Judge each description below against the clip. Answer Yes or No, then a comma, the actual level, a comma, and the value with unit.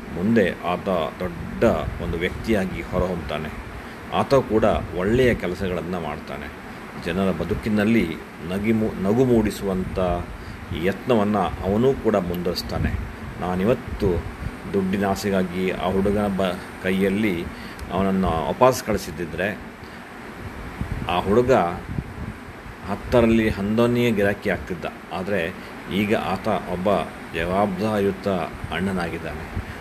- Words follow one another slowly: Yes, slow, 85 wpm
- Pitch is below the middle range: Yes, low, 100 Hz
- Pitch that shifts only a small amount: No, average, 3.3 semitones